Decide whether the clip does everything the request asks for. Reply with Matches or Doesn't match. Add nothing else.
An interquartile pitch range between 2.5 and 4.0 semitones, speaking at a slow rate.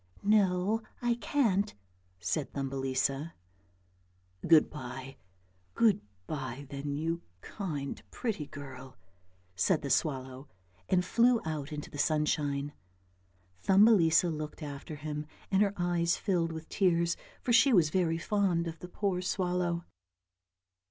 Doesn't match